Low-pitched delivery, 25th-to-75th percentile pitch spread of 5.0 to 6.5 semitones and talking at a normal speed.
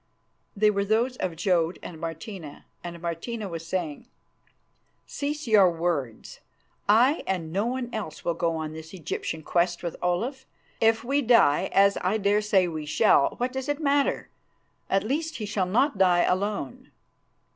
No: high, 195 Hz; wide, 5.5 semitones; average, 160 wpm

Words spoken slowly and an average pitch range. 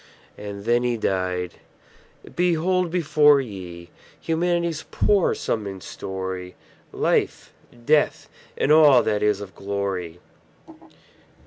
No: slow, 105 wpm; wide, 8.7 semitones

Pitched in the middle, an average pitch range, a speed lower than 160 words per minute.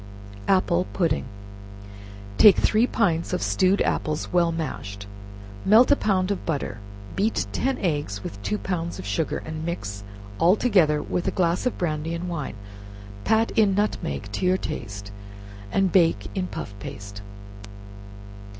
Yes: medium, 170 Hz; average, 4.6 semitones; average, 145 wpm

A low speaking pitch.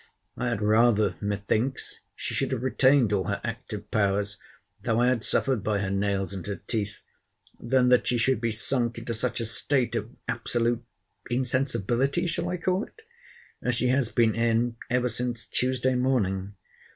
Yes: low, 115 Hz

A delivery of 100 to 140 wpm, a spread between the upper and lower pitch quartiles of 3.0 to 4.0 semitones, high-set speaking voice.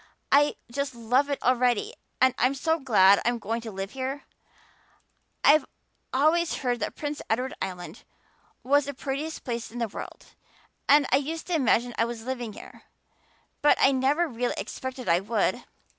No: average, 165 wpm; average, 3.4 semitones; very high, 260 Hz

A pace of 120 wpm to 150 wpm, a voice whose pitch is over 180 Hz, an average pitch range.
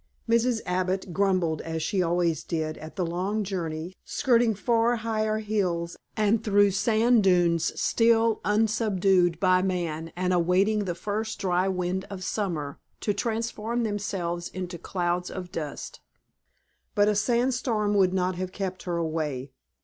Yes: average, 145 wpm; high, 190 Hz; average, 3.6 semitones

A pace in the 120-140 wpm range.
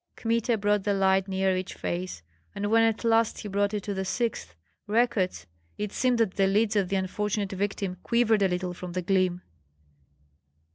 No: average, 185 wpm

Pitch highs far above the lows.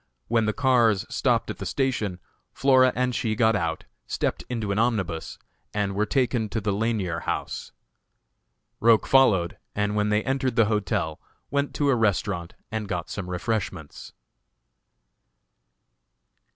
No: average, 3.8 semitones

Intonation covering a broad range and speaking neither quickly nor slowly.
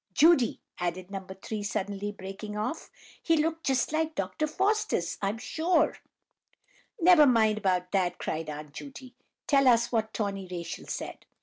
Yes: wide, 8.0 semitones; average, 145 wpm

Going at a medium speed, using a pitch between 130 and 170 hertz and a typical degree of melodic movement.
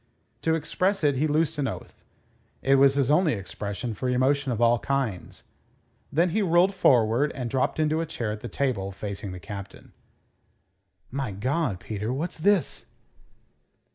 No: average, 160 wpm; low, 135 Hz; wide, 6.0 semitones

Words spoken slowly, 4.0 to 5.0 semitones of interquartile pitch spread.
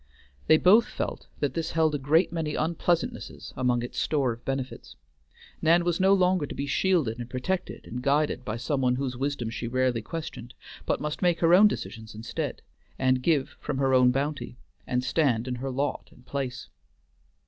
No: average, 185 wpm; average, 4.5 semitones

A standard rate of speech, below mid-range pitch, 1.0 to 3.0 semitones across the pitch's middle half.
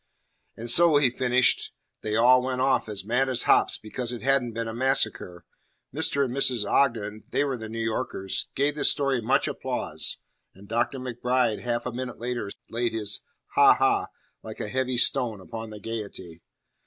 Yes: average, 180 wpm; low, 120 Hz; average, 2.7 semitones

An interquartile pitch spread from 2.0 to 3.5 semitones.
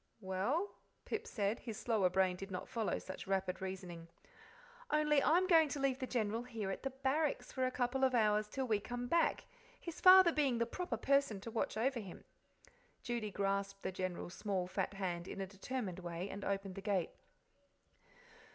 No: wide, 5.6 semitones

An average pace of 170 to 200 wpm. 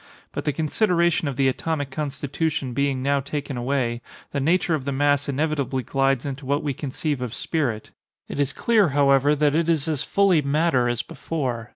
Yes: average, 185 wpm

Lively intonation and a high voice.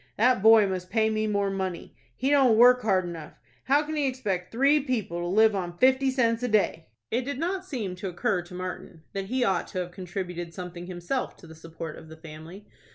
Yes: wide, 6.0 semitones; high, 195 Hz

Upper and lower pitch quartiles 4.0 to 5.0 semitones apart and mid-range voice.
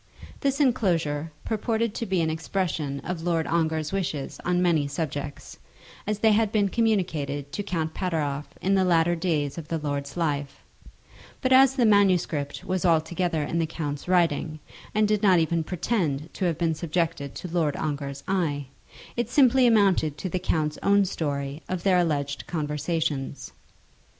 Yes: average, 4.3 semitones; medium, 165 Hz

